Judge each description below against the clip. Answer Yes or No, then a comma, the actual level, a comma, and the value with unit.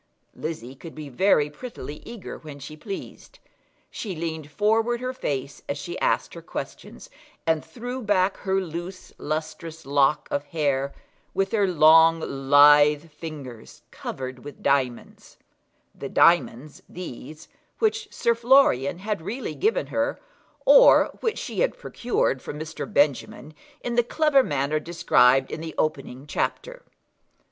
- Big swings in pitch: Yes, wide, 6.6 semitones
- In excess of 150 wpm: No, slow, 135 wpm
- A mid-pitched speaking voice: Yes, medium, 160 Hz